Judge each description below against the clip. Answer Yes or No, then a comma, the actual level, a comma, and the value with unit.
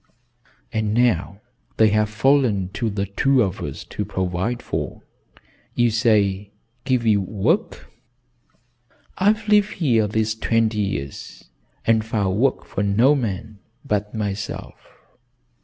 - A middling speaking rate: No, slow, 125 wpm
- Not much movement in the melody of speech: No, average, 3.3 semitones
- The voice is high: No, low, 110 Hz